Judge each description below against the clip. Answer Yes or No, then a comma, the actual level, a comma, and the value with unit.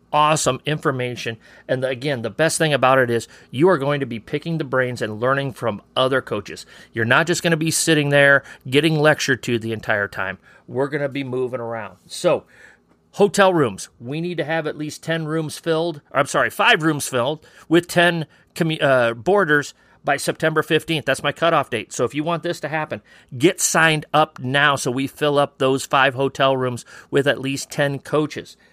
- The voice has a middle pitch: Yes, medium, 145 Hz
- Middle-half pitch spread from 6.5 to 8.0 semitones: No, average, 3.6 semitones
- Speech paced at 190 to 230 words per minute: Yes, fast, 205 wpm